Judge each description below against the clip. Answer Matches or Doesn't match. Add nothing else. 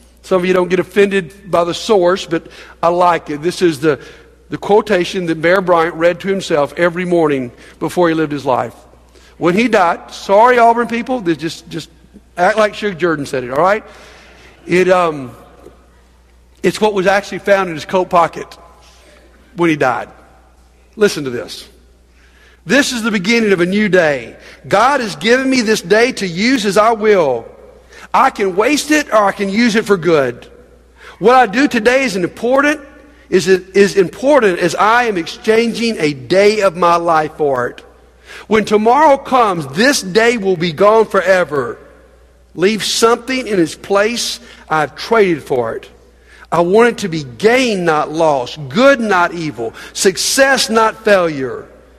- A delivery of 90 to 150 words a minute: Doesn't match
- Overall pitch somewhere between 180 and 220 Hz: Matches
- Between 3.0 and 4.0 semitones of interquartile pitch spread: Doesn't match